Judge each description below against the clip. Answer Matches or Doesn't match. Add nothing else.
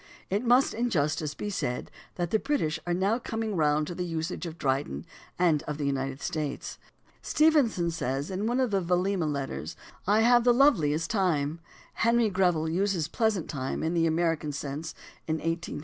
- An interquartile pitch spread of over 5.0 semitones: Matches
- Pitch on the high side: Doesn't match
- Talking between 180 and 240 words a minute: Matches